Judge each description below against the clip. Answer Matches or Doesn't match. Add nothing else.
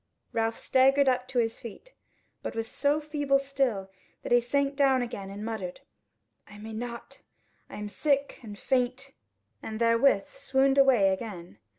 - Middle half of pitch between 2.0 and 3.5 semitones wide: Doesn't match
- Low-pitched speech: Doesn't match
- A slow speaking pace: Doesn't match